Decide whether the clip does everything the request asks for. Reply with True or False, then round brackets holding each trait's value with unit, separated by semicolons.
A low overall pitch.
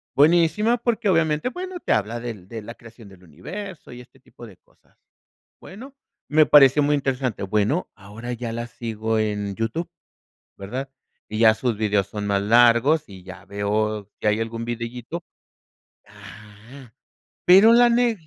True (115 Hz)